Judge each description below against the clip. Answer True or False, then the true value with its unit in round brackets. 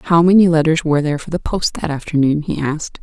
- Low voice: False (160 Hz)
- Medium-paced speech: False (240 wpm)